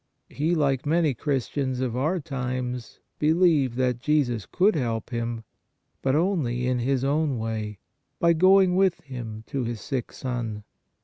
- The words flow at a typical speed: Yes, average, 145 wpm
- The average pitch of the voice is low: Yes, low, 130 Hz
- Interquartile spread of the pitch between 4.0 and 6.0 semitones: Yes, average, 4.4 semitones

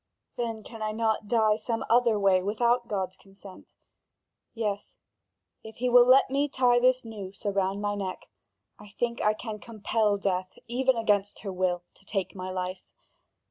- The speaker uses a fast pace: No, average, 165 wpm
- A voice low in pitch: No, high, 215 Hz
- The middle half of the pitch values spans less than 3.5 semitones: Yes, average, 3.1 semitones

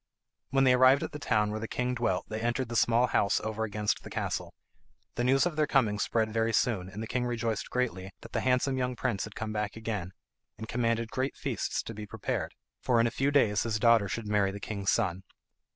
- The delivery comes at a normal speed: No, fast, 230 wpm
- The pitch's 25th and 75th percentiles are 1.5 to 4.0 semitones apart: Yes, average, 3.0 semitones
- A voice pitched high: No, low, 115 Hz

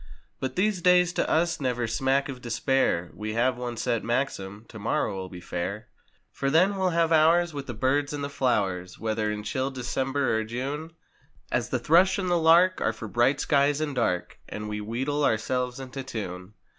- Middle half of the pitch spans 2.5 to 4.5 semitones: No, average, 5.2 semitones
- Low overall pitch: Yes, low, 130 Hz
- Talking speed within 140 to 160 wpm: No, average, 180 wpm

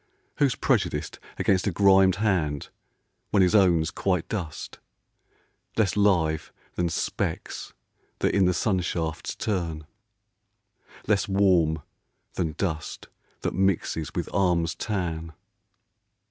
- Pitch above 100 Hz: No, very low, 90 Hz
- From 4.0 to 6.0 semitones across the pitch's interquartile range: No, average, 3.3 semitones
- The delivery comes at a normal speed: No, slow, 110 wpm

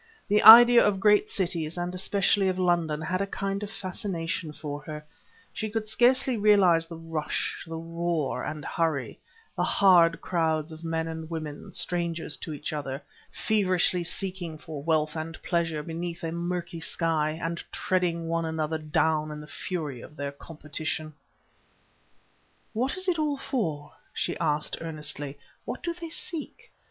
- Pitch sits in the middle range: Yes, medium, 165 Hz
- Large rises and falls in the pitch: No, average, 3.4 semitones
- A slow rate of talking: No, average, 155 wpm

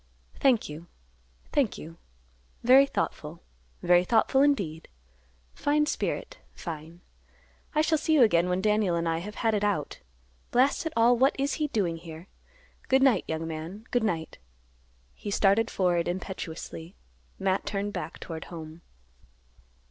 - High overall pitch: Yes, high, 195 Hz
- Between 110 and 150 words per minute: Yes, average, 145 wpm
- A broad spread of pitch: Yes, wide, 6.6 semitones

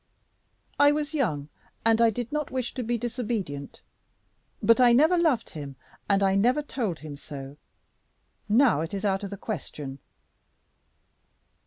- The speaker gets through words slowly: No, average, 150 wpm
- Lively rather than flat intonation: Yes, wide, 7.6 semitones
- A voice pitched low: No, high, 225 Hz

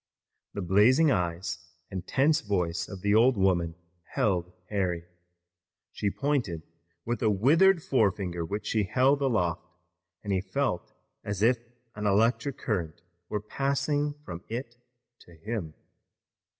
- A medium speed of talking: No, slow, 130 wpm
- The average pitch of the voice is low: Yes, low, 105 Hz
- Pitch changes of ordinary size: No, wide, 6.2 semitones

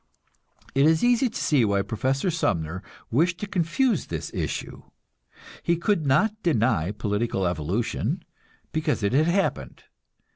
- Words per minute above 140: No, slow, 135 wpm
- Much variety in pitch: Yes, wide, 8.9 semitones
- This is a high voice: No, medium, 140 Hz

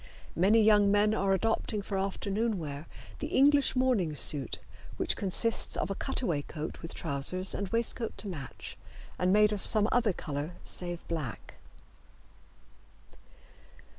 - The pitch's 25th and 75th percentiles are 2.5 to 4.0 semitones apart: No, average, 4.7 semitones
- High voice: Yes, high, 195 Hz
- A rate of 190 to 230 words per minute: No, slow, 135 wpm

